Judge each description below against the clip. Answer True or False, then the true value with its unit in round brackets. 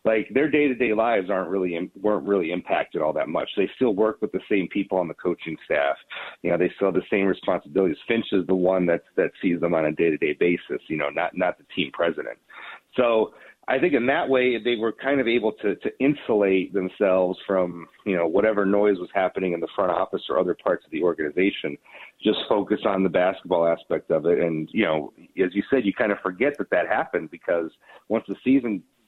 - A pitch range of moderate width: True (4.0 semitones)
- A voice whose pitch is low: True (95 Hz)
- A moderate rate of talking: False (230 wpm)